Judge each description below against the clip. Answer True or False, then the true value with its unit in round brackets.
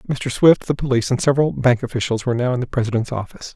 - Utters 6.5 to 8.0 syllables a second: True (7.5 syllables/s)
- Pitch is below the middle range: True (125 Hz)